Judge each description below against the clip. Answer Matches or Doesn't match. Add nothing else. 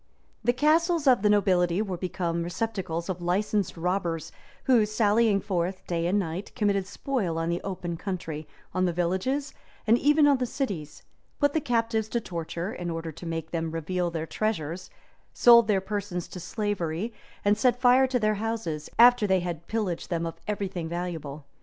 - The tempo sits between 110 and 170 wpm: Doesn't match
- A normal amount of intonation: Matches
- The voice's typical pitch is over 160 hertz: Matches